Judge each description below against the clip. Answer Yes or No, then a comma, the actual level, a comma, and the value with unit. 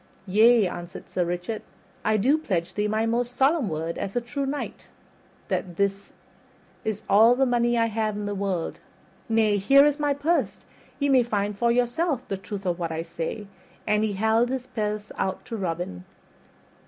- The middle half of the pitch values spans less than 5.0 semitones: Yes, average, 4.0 semitones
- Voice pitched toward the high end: Yes, high, 215 Hz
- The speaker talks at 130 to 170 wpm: No, average, 180 wpm